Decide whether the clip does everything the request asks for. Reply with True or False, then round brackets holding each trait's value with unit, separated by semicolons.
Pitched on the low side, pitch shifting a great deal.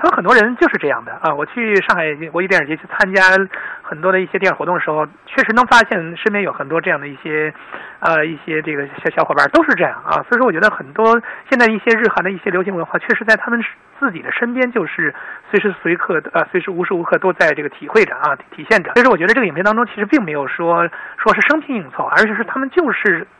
False (205 Hz; 5.9 semitones)